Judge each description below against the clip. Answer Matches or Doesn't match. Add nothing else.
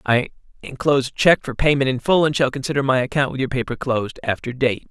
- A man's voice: Matches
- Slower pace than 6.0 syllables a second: Doesn't match